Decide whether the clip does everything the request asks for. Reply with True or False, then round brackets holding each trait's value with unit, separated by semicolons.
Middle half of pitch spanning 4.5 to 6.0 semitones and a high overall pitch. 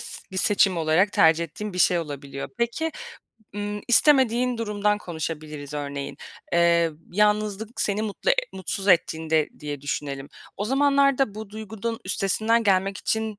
True (5.4 semitones; 200 Hz)